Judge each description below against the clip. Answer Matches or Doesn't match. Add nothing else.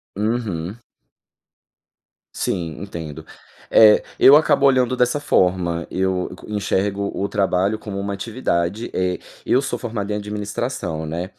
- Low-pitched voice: Matches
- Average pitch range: Matches